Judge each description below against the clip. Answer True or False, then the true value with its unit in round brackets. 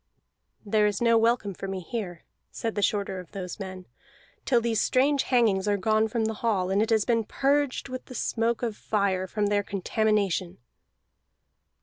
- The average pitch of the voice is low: False (215 Hz)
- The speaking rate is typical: True (180 wpm)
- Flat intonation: False (3.0 semitones)